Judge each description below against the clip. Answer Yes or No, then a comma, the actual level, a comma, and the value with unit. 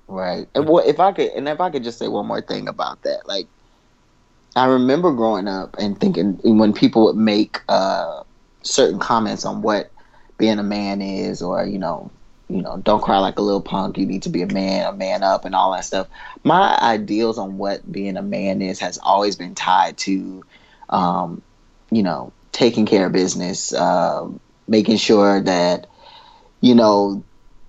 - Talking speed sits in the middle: Yes, average, 190 wpm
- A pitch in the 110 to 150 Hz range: No, low, 100 Hz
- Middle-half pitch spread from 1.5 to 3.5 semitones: Yes, narrow, 2.4 semitones